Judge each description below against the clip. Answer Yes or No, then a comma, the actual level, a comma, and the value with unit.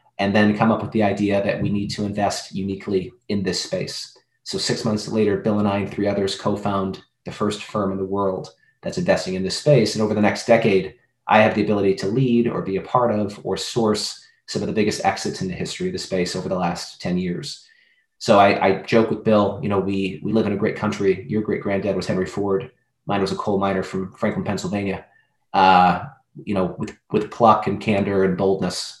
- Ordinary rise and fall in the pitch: No, narrow, 1.9 semitones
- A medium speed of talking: No, fast, 230 wpm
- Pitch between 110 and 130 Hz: No, low, 100 Hz